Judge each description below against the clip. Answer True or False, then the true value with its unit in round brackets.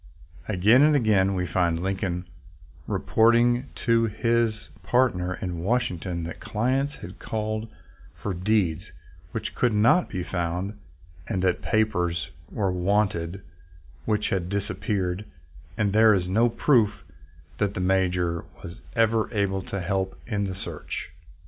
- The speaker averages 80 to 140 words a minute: True (135 wpm)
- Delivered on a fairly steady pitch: False (3.6 semitones)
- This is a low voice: True (100 Hz)